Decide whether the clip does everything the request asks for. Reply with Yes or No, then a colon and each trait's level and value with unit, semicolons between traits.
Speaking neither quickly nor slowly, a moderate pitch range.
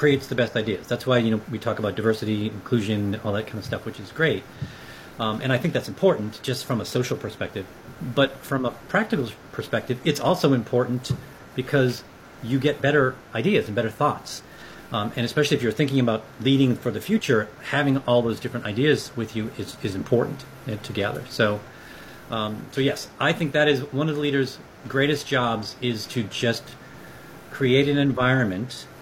Yes: average, 190 wpm; average, 3.8 semitones